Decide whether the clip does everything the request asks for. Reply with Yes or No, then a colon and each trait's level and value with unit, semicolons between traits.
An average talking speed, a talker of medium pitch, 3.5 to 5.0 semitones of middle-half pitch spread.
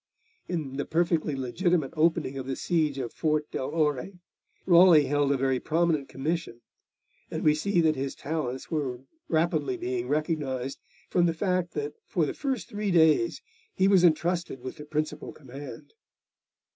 Yes: average, 160 wpm; medium, 155 Hz; average, 3.8 semitones